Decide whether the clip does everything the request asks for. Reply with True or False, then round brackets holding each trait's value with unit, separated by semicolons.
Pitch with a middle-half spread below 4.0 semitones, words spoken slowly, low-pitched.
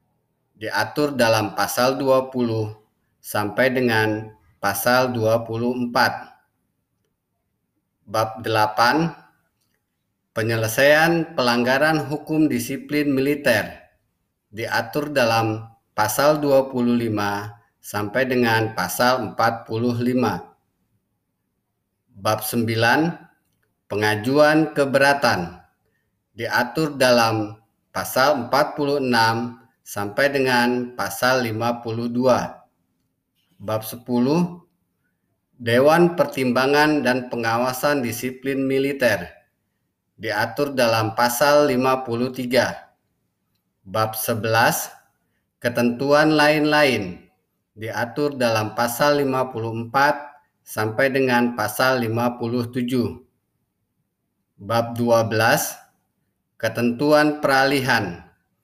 True (3.4 semitones; 65 wpm; 120 Hz)